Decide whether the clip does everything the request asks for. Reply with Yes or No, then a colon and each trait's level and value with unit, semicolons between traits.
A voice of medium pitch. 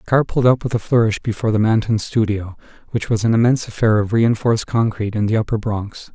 No: low, 110 Hz